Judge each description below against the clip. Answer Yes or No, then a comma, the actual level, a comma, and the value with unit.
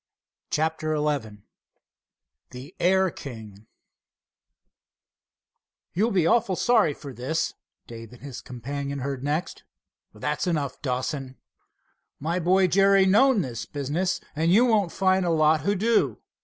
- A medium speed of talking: No, slow, 125 wpm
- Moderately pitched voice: Yes, medium, 155 Hz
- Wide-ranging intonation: Yes, wide, 5.8 semitones